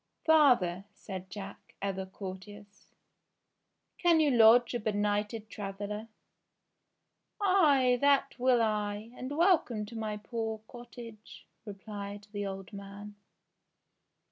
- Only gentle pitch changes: No, average, 3.3 semitones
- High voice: Yes, high, 215 Hz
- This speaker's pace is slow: Yes, slow, 115 wpm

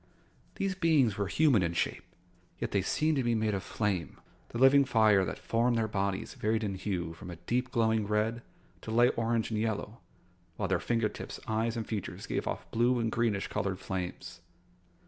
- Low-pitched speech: Yes, low, 110 Hz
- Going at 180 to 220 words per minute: Yes, average, 190 wpm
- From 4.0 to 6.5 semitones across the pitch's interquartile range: No, average, 3.2 semitones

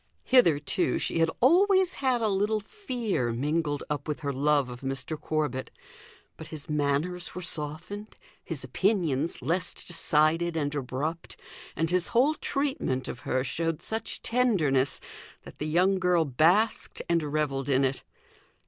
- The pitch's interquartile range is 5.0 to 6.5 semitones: Yes, average, 5.3 semitones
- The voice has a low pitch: No, medium, 160 Hz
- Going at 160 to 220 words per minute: No, average, 145 wpm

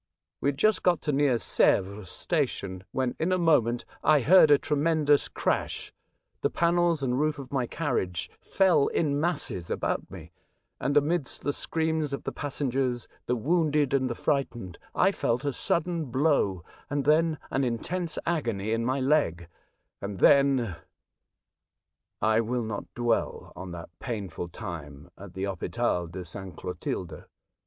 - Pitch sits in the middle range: No, low, 130 Hz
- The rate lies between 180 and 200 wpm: No, average, 155 wpm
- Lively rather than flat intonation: Yes, wide, 6.8 semitones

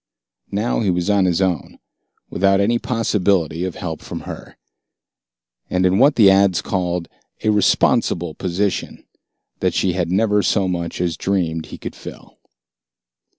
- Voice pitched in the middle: No, very low, 95 Hz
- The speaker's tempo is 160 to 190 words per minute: No, average, 150 wpm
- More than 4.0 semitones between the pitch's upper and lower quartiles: No, narrow, 2.6 semitones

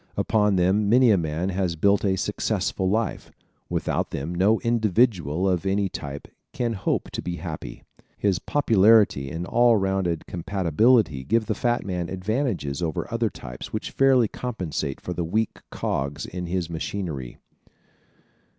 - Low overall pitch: Yes, very low, 95 Hz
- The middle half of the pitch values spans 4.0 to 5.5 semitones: Yes, average, 4.7 semitones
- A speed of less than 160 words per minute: Yes, average, 150 wpm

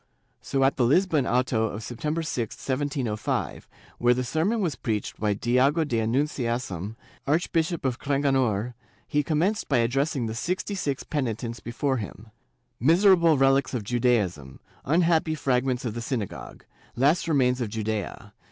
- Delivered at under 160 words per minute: Yes, average, 150 wpm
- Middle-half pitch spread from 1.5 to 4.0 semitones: No, average, 4.5 semitones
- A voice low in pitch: Yes, low, 130 Hz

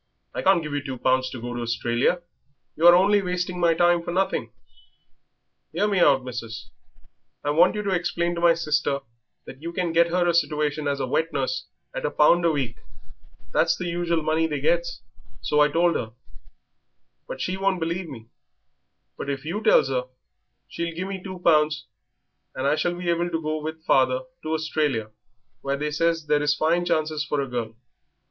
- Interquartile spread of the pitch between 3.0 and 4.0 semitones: Yes, average, 3.5 semitones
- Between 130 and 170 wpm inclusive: No, average, 195 wpm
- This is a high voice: No, medium, 160 Hz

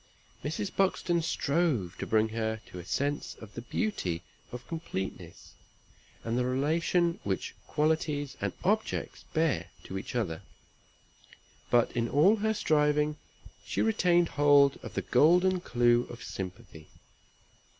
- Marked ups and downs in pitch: Yes, wide, 6.8 semitones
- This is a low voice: No, medium, 145 Hz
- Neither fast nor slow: No, slow, 130 wpm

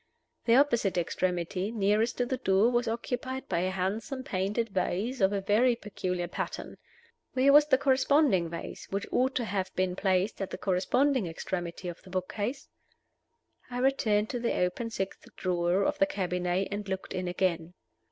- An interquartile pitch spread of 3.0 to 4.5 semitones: No, average, 5.0 semitones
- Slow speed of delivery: No, average, 170 wpm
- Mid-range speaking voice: No, high, 200 Hz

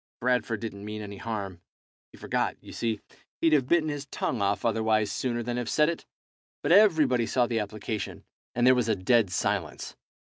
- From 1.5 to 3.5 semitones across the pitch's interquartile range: Yes, average, 3.2 semitones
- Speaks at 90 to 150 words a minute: No, average, 185 wpm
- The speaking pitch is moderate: No, low, 115 Hz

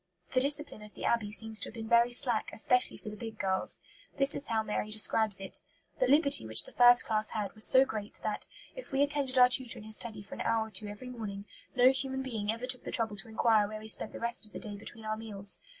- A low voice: No, high, 225 Hz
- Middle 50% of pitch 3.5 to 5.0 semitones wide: No, average, 2.9 semitones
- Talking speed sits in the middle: No, fast, 260 wpm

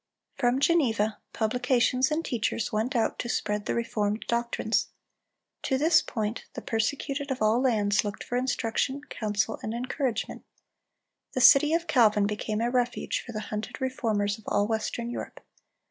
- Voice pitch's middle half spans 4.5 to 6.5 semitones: No, average, 3.4 semitones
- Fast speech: No, average, 155 wpm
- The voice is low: No, high, 235 Hz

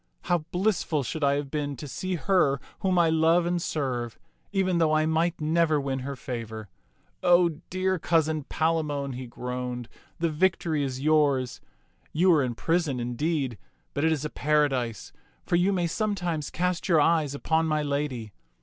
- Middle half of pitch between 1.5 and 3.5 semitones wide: No, average, 3.9 semitones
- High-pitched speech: No, medium, 155 Hz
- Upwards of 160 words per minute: Yes, average, 175 wpm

